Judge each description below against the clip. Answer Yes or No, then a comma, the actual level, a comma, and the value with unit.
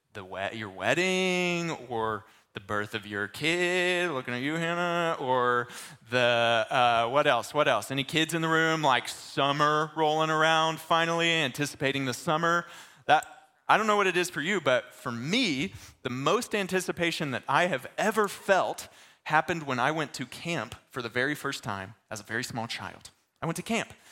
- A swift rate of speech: No, average, 180 wpm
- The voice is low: No, medium, 150 Hz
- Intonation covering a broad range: Yes, wide, 5.8 semitones